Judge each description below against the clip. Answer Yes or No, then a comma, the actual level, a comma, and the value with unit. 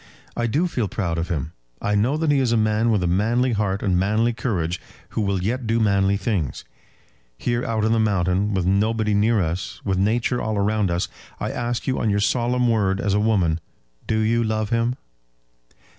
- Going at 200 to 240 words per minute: Yes, fast, 205 wpm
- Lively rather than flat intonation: No, average, 3.2 semitones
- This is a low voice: Yes, low, 110 Hz